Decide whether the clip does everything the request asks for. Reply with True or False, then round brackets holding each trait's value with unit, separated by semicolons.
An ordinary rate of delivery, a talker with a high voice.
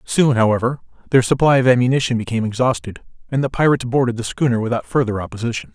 False (180 wpm; 120 Hz)